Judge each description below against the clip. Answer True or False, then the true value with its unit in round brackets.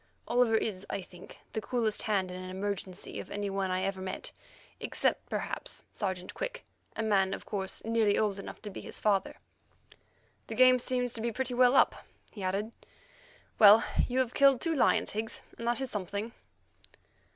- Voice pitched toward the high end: True (210 Hz)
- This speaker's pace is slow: False (180 wpm)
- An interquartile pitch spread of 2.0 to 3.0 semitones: False (3.8 semitones)